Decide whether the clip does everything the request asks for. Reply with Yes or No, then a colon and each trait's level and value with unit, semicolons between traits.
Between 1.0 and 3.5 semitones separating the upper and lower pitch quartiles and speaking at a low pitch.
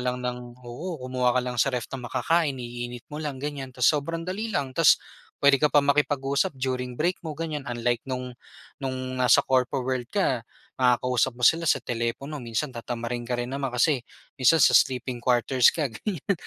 Yes: average, 2.7 semitones; low, 130 Hz